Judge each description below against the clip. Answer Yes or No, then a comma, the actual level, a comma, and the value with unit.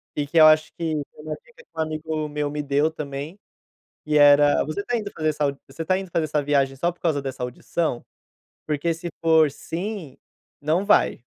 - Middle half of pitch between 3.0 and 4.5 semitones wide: No, narrow, 2.4 semitones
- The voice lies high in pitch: No, medium, 155 Hz